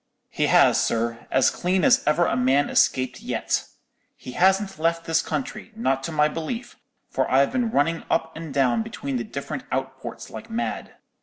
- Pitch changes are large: Yes, wide, 6.0 semitones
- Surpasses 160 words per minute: Yes, average, 175 wpm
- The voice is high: No, medium, 160 Hz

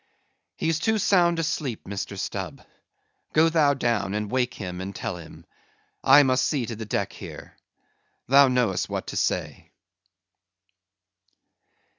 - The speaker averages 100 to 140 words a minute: Yes, slow, 135 wpm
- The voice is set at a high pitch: No, low, 125 Hz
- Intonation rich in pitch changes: Yes, wide, 7.1 semitones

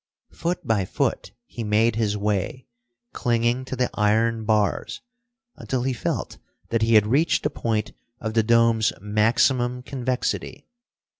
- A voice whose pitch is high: No, low, 115 Hz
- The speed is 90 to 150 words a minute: Yes, average, 140 wpm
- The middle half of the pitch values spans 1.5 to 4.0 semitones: Yes, narrow, 2.6 semitones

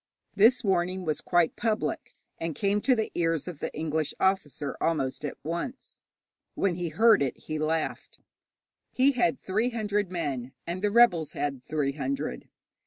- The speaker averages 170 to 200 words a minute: No, average, 160 wpm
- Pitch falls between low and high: Yes, medium, 175 Hz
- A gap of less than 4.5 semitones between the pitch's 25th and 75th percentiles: No, average, 5.1 semitones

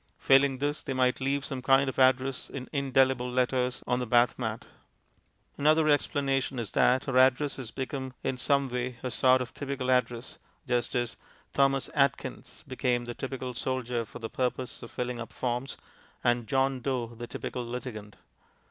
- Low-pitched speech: Yes, low, 130 Hz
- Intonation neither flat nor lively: No, narrow, 1.6 semitones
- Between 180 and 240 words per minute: No, average, 170 wpm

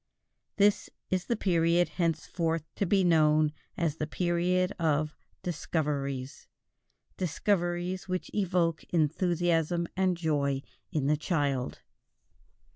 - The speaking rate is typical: No, slow, 105 wpm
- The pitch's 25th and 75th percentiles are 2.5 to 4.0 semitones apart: Yes, average, 2.9 semitones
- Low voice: No, medium, 170 Hz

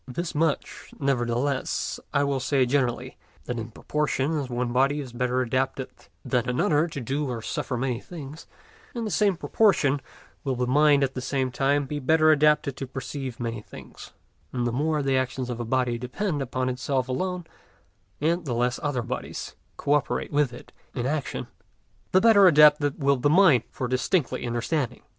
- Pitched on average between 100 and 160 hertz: Yes, low, 135 Hz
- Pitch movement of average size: Yes, average, 3.1 semitones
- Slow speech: No, average, 175 wpm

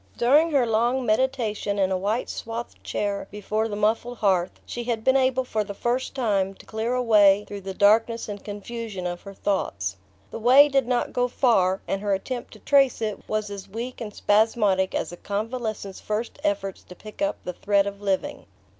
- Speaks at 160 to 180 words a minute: No, average, 200 wpm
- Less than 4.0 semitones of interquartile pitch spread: Yes, average, 3.4 semitones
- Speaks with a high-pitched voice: Yes, high, 215 Hz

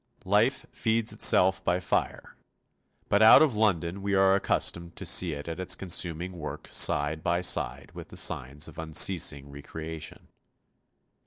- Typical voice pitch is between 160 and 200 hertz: No, very low, 85 Hz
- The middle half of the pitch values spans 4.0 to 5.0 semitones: No, average, 3.5 semitones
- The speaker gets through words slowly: No, average, 155 wpm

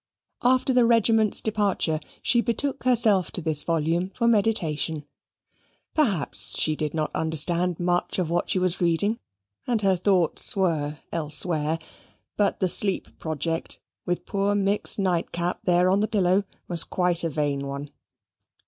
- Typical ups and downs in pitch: Yes, average, 4.2 semitones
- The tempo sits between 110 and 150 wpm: Yes, average, 145 wpm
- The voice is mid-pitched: Yes, medium, 180 Hz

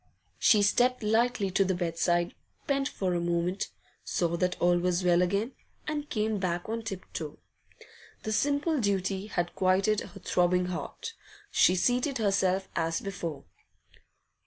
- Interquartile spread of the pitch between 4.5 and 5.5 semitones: No, average, 3.8 semitones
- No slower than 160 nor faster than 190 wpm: No, average, 145 wpm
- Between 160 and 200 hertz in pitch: Yes, high, 190 Hz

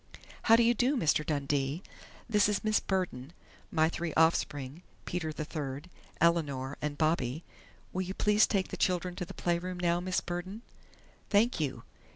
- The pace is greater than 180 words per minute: No, average, 165 wpm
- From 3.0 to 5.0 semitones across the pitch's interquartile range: Yes, average, 4.0 semitones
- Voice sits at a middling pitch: Yes, medium, 170 Hz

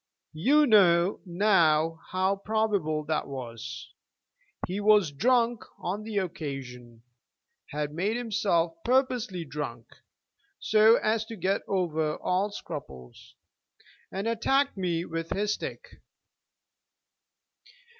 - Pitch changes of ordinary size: No, wide, 5.8 semitones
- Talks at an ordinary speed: No, slow, 105 wpm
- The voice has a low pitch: No, medium, 185 Hz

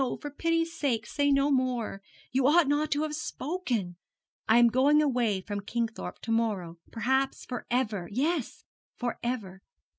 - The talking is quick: No, average, 155 wpm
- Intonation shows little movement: No, average, 4.5 semitones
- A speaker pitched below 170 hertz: No, very high, 250 Hz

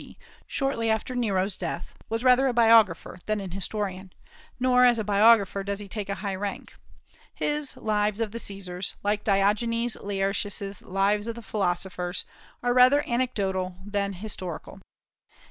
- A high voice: Yes, high, 205 Hz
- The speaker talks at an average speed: Yes, average, 150 wpm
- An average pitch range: Yes, average, 3.0 semitones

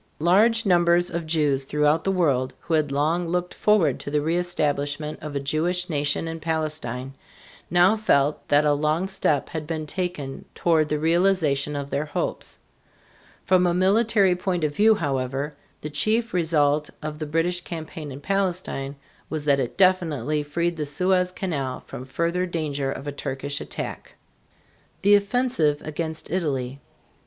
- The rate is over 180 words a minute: No, average, 155 wpm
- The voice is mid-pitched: Yes, medium, 155 Hz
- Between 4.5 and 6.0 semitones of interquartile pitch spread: No, average, 3.5 semitones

